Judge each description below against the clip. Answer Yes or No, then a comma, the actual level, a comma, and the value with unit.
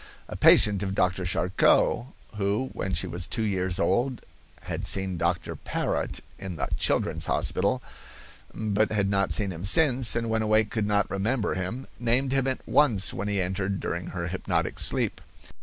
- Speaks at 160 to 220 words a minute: Yes, average, 170 wpm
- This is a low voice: Yes, low, 100 Hz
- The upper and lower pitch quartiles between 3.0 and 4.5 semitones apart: Yes, average, 3.4 semitones